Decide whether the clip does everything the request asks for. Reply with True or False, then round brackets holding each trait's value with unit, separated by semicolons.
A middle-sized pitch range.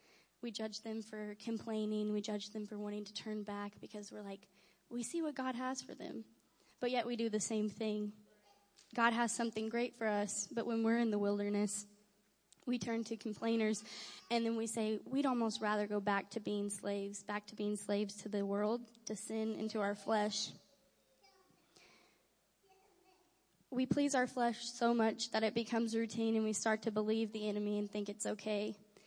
False (1.9 semitones)